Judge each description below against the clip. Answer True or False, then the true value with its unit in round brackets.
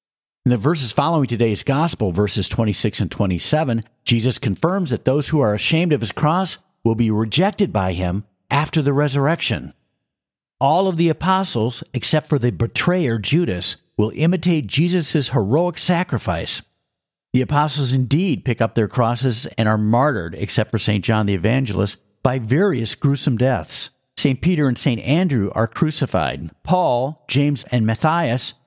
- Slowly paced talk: False (155 wpm)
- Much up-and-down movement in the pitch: True (5.9 semitones)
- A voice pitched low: True (130 Hz)